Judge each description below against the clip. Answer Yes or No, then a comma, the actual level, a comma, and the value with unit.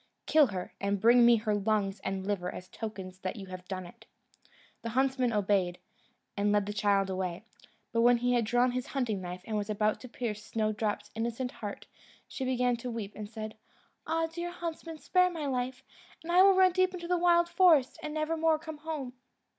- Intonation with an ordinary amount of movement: No, wide, 6.9 semitones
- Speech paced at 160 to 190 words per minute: No, average, 200 wpm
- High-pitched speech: Yes, high, 235 Hz